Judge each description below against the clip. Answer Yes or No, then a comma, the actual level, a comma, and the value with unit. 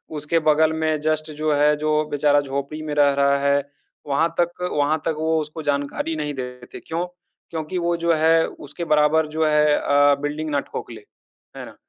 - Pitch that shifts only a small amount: Yes, narrow, 1.8 semitones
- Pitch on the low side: No, medium, 150 Hz